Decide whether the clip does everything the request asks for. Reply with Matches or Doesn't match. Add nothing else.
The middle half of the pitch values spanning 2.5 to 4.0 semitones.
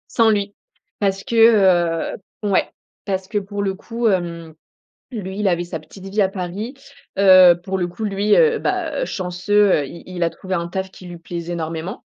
Matches